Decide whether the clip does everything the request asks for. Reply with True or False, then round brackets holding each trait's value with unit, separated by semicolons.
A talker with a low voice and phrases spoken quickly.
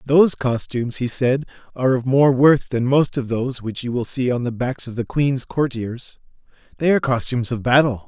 True (130 Hz; 210 wpm)